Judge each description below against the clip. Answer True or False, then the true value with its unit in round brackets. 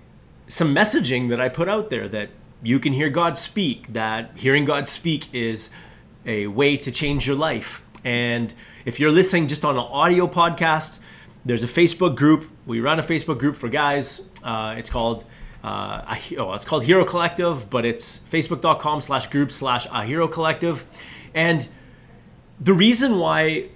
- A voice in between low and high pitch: True (145 Hz)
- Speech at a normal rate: True (165 wpm)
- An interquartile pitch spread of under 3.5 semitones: False (5.2 semitones)